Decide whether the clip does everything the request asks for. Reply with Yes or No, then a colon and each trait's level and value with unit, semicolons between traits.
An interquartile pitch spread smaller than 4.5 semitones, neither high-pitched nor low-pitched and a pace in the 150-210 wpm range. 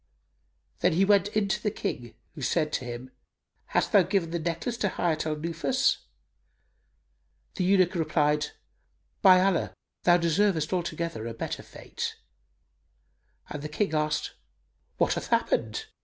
No: average, 4.1 semitones; medium, 170 Hz; average, 140 wpm